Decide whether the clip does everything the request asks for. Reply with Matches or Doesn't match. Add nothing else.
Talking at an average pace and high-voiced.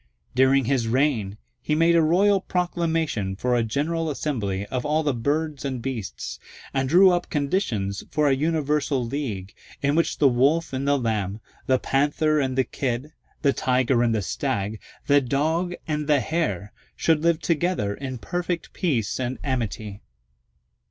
Doesn't match